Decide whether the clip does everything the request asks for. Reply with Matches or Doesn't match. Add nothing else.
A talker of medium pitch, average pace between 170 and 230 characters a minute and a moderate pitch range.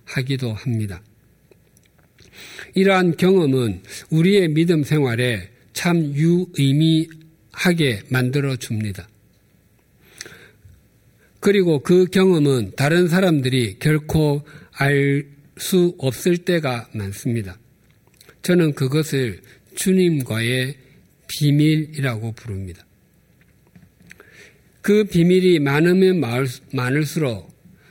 Doesn't match